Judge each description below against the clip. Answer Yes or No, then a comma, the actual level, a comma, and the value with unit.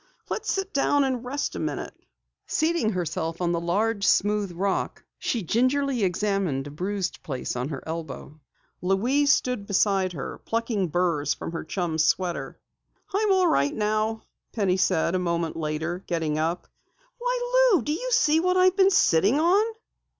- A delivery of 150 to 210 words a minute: Yes, average, 160 wpm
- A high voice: Yes, high, 195 Hz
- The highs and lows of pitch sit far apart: Yes, wide, 8.7 semitones